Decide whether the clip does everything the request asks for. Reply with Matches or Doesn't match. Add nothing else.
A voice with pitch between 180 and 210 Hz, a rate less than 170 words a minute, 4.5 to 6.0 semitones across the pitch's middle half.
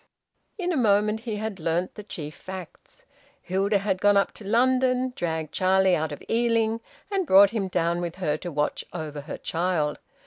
Doesn't match